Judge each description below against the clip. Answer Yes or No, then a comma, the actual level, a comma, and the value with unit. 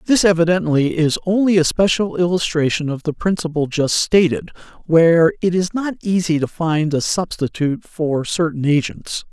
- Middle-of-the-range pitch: Yes, medium, 165 Hz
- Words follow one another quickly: No, average, 155 wpm